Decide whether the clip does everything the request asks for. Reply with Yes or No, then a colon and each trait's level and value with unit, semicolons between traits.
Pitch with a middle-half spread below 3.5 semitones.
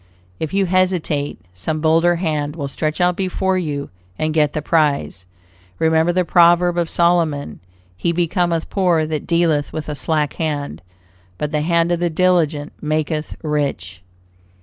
Yes: narrow, 2.6 semitones